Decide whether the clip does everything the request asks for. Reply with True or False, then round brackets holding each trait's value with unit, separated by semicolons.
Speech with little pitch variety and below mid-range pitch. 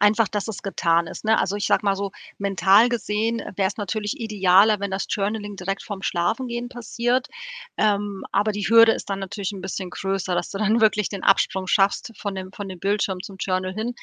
False (2.1 semitones; 200 Hz)